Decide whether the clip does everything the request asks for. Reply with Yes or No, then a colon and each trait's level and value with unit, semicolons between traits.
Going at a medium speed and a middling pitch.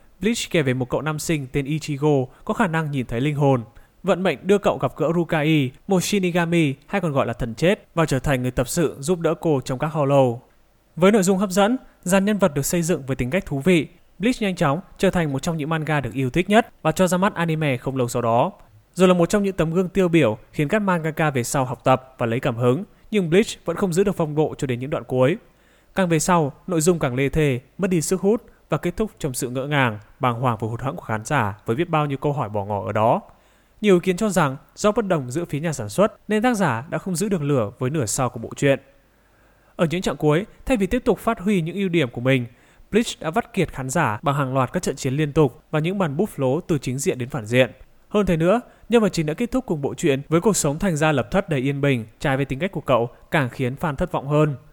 No: fast, 275 wpm; medium, 155 Hz